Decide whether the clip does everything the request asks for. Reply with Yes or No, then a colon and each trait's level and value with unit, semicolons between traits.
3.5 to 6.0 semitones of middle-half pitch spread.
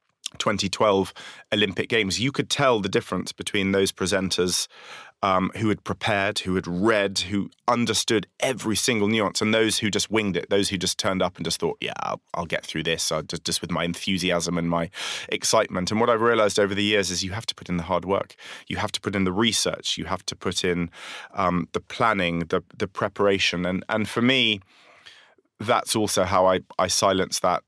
No: average, 3.0 semitones